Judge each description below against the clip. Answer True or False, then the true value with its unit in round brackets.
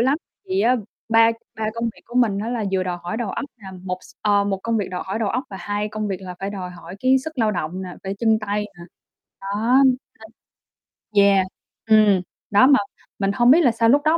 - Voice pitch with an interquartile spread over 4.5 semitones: False (3.2 semitones)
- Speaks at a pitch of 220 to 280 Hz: False (210 Hz)